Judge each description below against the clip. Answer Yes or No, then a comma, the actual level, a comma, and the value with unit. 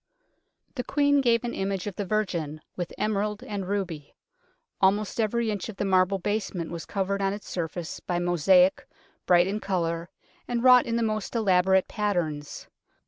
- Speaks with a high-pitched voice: Yes, high, 195 Hz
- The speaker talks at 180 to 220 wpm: No, average, 165 wpm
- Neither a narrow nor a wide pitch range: Yes, average, 3.3 semitones